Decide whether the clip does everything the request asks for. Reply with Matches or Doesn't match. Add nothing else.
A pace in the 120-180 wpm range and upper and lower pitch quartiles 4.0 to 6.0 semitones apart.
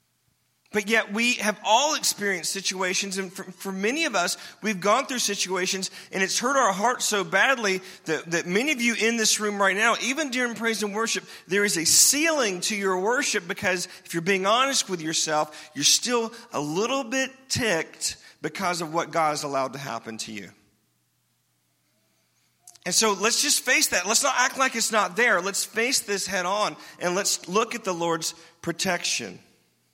Doesn't match